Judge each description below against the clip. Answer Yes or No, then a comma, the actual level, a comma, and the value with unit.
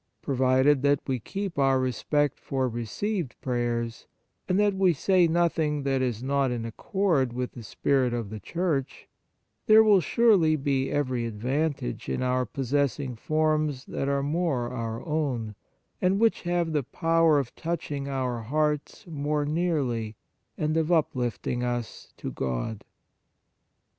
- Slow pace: No, average, 145 wpm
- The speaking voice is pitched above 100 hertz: Yes, medium, 140 Hz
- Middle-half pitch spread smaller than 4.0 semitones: No, average, 4.6 semitones